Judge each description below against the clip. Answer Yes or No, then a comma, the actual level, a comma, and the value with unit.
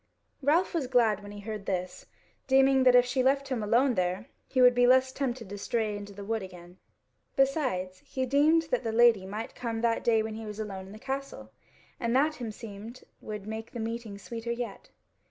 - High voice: Yes, high, 230 Hz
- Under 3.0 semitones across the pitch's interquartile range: No, average, 4.0 semitones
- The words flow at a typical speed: No, fast, 210 wpm